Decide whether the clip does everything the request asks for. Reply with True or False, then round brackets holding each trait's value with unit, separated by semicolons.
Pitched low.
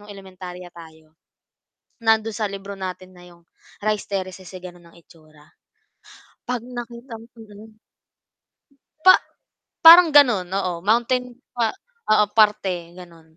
False (200 Hz)